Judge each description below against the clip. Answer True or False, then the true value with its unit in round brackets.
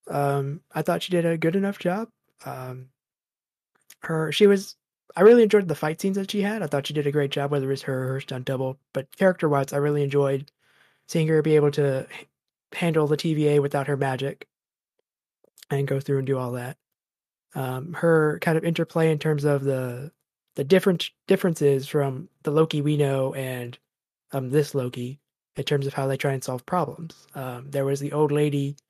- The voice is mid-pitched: True (145 Hz)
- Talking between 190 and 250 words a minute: True (200 wpm)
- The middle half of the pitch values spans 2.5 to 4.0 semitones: True (3.0 semitones)